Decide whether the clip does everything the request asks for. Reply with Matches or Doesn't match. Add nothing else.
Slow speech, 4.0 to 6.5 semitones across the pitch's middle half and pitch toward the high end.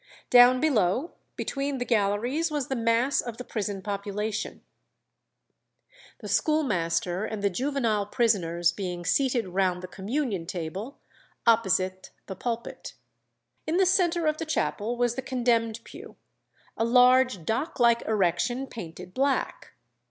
Matches